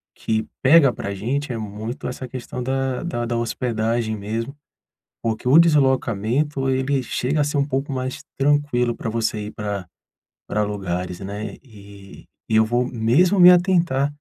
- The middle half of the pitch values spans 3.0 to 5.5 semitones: Yes, average, 4.1 semitones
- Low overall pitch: Yes, low, 125 Hz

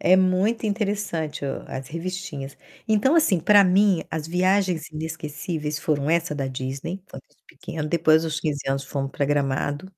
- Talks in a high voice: No, medium, 160 Hz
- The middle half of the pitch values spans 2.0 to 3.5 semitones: No, average, 4.3 semitones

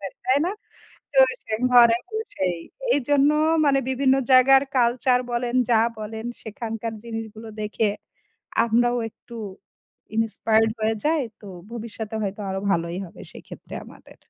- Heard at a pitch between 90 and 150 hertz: No, high, 230 Hz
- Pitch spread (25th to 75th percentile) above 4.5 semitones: No, average, 2.8 semitones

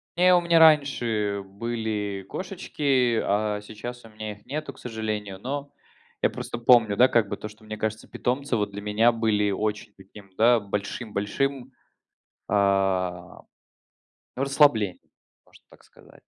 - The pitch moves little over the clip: No, average, 3.5 semitones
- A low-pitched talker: Yes, low, 110 Hz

